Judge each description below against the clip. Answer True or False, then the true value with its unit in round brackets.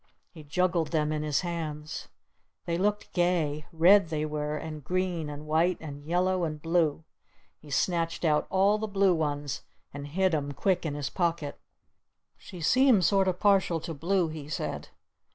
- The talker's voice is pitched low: False (165 Hz)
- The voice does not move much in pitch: False (3.4 semitones)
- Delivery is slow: False (170 wpm)